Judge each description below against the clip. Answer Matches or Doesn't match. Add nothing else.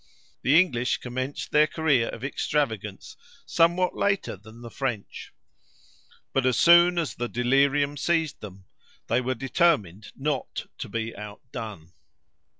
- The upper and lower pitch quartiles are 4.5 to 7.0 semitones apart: Matches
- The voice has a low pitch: Matches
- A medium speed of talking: Doesn't match